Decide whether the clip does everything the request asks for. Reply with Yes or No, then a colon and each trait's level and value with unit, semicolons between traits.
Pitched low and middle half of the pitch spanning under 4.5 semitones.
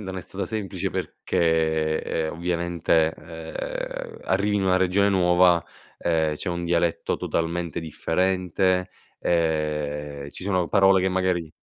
Yes: very low, 85 Hz; narrow, 2.6 semitones